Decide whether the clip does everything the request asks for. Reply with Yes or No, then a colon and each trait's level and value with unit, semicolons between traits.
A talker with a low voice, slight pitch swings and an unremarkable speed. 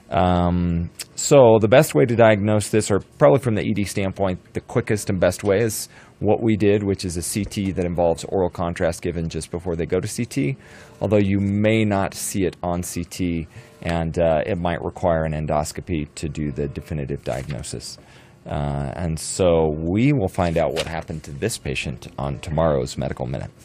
No: very low, 90 Hz; average, 4.6 semitones; average, 190 wpm